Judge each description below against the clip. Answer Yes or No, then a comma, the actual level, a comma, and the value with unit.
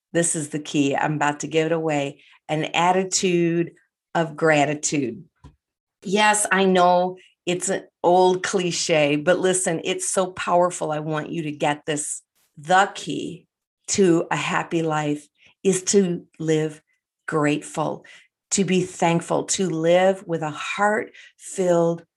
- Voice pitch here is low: No, medium, 170 Hz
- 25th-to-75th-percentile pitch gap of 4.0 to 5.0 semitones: No, average, 3.1 semitones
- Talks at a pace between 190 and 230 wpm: No, average, 140 wpm